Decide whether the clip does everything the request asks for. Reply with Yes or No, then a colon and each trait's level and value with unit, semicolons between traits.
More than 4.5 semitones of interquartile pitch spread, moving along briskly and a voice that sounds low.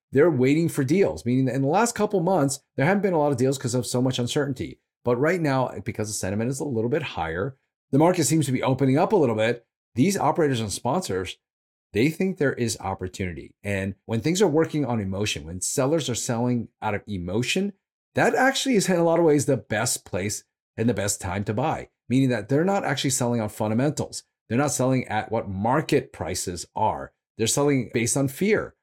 Yes: average, 5.2 semitones; fast, 220 wpm; low, 130 Hz